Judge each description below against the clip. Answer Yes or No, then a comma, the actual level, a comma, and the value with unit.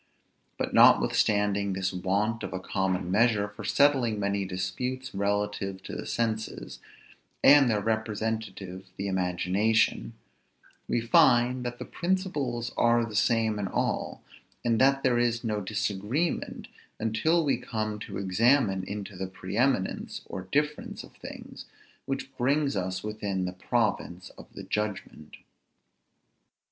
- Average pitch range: Yes, average, 3.9 semitones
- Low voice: Yes, low, 110 Hz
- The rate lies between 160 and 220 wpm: No, slow, 135 wpm